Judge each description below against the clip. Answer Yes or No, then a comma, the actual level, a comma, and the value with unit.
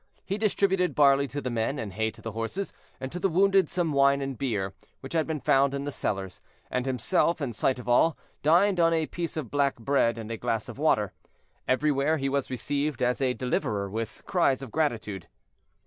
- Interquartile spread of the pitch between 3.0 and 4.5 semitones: No, average, 5.3 semitones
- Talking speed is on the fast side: Yes, fast, 210 wpm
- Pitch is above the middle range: No, medium, 140 Hz